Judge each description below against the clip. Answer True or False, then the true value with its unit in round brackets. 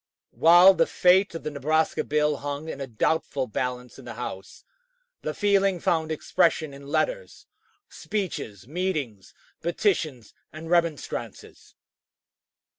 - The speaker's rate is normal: False (120 wpm)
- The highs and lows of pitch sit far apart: False (4.4 semitones)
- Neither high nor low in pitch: True (155 Hz)